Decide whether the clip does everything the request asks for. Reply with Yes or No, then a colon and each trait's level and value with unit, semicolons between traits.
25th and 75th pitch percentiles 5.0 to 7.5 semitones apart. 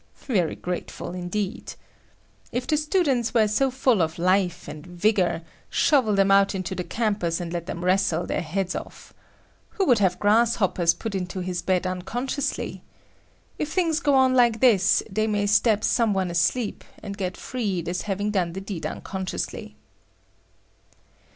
No: average, 4.5 semitones